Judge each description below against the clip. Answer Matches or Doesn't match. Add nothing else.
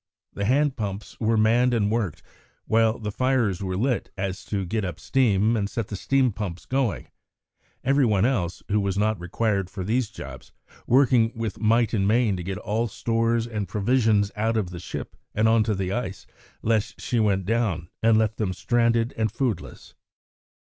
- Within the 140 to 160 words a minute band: Doesn't match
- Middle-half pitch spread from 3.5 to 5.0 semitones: Doesn't match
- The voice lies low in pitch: Matches